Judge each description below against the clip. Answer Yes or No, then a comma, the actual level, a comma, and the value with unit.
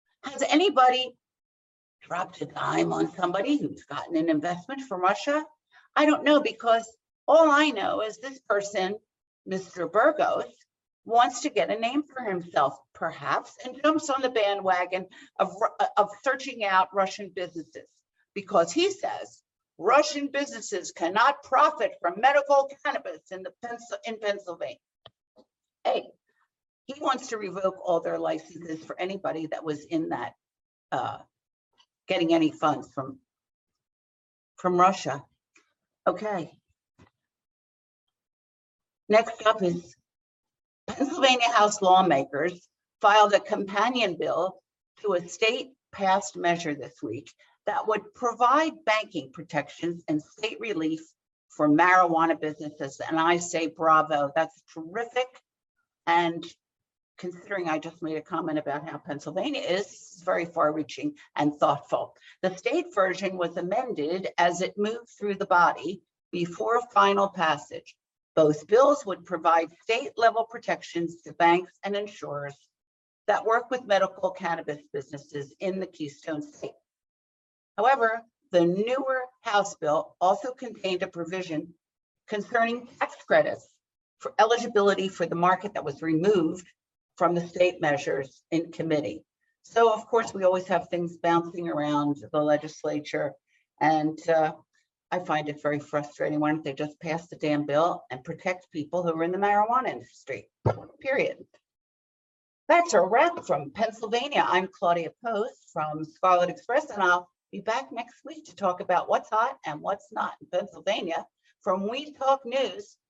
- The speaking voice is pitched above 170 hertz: Yes, medium, 185 Hz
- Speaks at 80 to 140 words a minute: Yes, slow, 135 wpm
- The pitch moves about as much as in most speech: No, wide, 6.5 semitones